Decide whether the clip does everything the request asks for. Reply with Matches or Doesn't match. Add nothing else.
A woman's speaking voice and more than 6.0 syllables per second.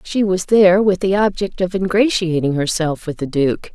Doesn't match